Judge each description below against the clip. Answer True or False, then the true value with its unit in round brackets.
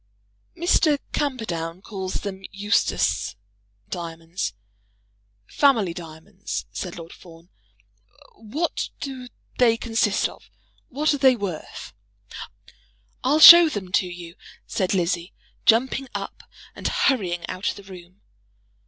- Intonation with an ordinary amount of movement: False (6.6 semitones)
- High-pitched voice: True (200 Hz)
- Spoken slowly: True (110 wpm)